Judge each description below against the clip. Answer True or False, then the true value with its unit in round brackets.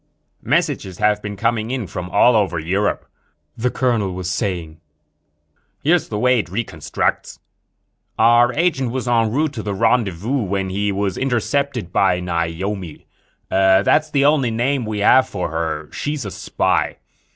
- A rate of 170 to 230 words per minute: False (150 wpm)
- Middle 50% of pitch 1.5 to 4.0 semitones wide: False (5.0 semitones)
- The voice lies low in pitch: True (105 Hz)